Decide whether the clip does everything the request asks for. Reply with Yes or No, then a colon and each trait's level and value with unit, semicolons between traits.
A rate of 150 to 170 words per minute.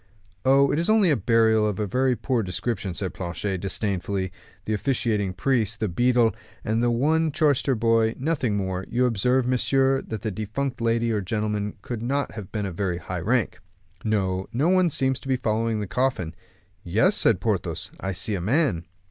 No: average, 185 wpm